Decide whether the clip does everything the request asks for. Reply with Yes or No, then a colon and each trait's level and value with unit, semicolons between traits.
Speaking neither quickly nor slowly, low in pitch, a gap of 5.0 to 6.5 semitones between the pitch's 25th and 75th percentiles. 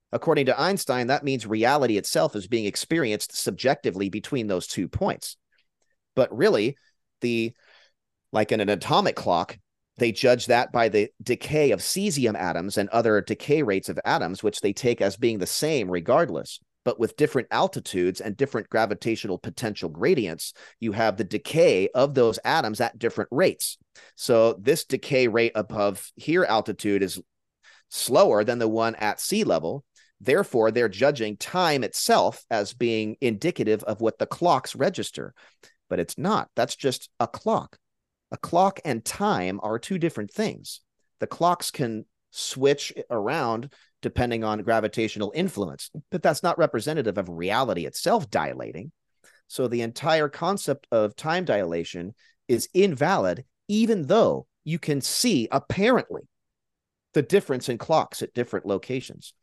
Yes: average, 150 wpm; low, 120 Hz; wide, 5.4 semitones